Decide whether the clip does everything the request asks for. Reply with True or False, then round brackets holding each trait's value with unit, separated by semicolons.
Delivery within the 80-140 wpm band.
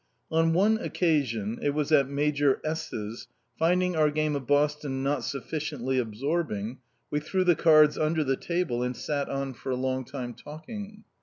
False (170 wpm)